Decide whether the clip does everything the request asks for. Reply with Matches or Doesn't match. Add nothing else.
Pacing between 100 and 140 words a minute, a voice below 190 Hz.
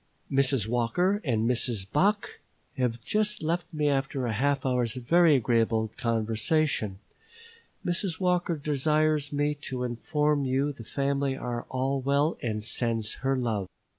Matches